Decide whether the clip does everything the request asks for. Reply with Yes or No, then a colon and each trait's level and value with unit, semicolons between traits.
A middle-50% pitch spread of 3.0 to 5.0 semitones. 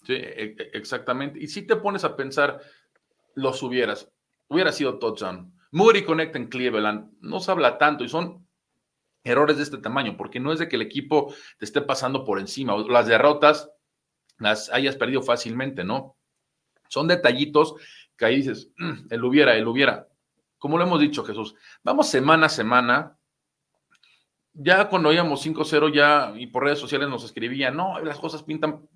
Yes: average, 3.4 semitones